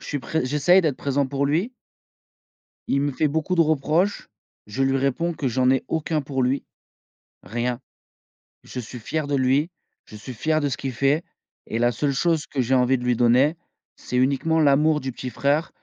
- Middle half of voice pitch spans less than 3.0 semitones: No, average, 3.3 semitones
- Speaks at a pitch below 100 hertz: No, medium, 140 Hz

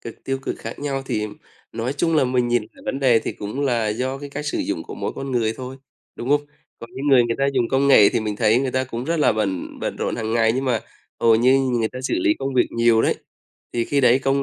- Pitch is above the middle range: No, low, 125 Hz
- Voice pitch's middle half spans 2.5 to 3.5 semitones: Yes, average, 2.9 semitones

